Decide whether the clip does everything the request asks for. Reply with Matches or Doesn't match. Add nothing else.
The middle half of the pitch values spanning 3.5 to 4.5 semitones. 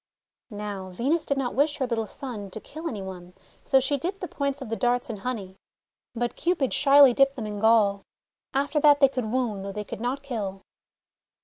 Doesn't match